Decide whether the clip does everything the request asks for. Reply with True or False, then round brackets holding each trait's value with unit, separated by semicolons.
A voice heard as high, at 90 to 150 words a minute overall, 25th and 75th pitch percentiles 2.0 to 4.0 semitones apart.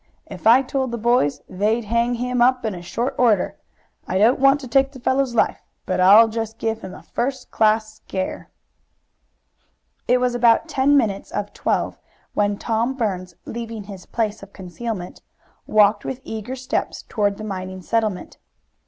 False (225 Hz; 160 wpm; 3.4 semitones)